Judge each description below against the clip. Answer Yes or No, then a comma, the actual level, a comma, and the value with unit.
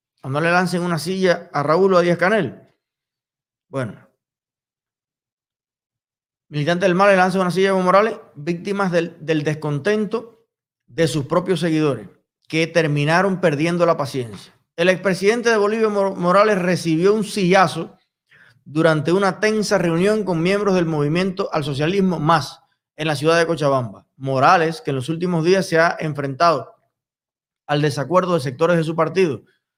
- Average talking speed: Yes, average, 150 wpm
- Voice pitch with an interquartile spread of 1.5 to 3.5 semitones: No, average, 4.0 semitones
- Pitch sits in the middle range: Yes, medium, 170 Hz